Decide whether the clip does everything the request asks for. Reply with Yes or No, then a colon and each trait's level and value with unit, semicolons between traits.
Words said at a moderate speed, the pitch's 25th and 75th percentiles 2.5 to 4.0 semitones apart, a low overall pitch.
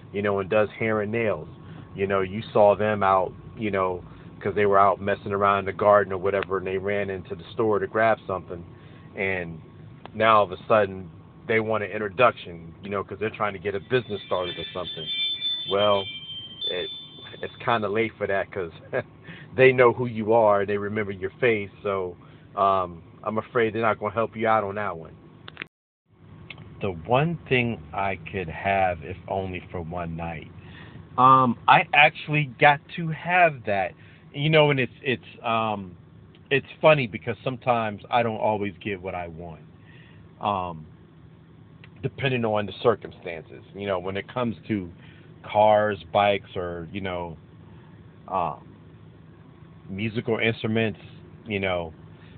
Yes: average, 165 wpm; average, 3.5 semitones; low, 105 Hz